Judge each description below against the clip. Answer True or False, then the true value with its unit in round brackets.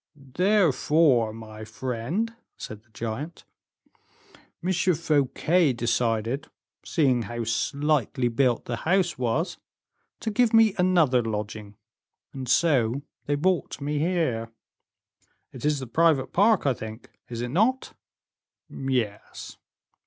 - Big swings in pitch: True (6.4 semitones)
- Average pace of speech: False (115 wpm)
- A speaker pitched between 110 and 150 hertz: True (135 Hz)